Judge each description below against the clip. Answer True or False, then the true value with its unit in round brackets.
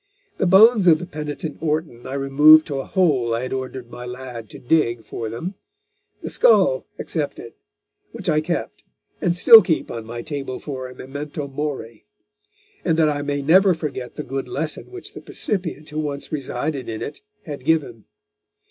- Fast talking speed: False (175 wpm)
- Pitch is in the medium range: True (145 Hz)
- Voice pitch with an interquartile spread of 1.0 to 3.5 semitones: False (4.0 semitones)